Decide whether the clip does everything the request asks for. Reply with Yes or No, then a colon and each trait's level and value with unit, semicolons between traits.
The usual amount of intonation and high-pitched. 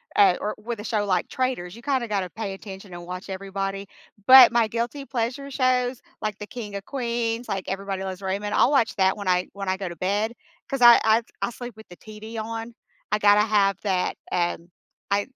Yes: average, 3.5 semitones; high, 210 Hz